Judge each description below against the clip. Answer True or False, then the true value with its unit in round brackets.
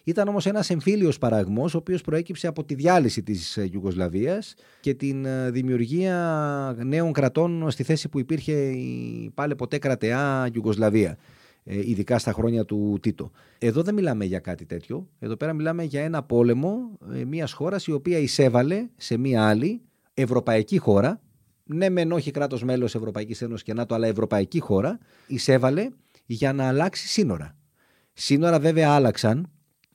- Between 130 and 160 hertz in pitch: True (135 Hz)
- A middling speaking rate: True (150 wpm)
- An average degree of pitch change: False (6.3 semitones)